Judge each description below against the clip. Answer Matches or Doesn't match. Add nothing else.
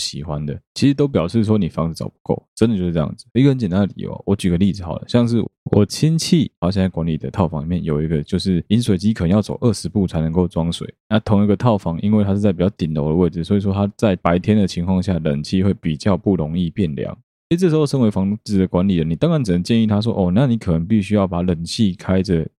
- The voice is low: Matches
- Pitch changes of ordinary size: Matches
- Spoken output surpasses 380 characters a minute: Matches